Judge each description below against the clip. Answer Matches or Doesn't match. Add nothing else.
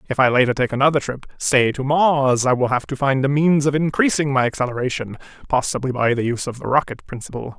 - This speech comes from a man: Matches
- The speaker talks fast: Matches